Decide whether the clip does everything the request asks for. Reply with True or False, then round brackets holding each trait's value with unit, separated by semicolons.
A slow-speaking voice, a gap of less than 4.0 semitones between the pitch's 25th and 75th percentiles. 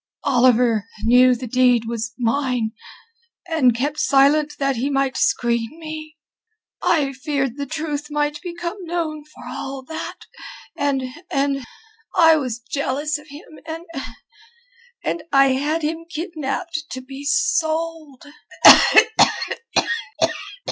True (115 wpm; 3.4 semitones)